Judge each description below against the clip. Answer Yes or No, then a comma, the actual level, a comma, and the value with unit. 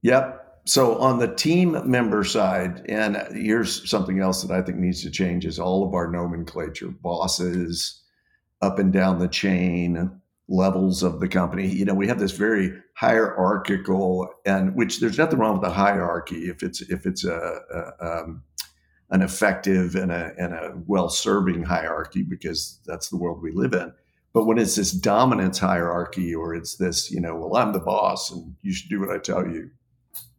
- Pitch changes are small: Yes, narrow, 2.1 semitones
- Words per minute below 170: No, average, 185 wpm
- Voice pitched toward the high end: No, very low, 95 Hz